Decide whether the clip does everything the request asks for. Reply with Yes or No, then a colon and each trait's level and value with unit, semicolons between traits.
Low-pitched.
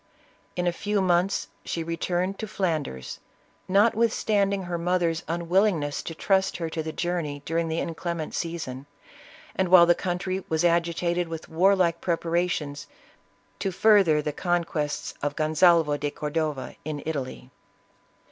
No: medium, 170 Hz